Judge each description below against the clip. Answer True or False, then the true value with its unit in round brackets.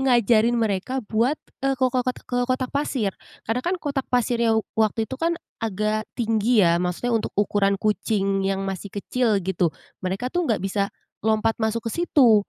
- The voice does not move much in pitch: False (3.7 semitones)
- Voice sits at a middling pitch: False (225 Hz)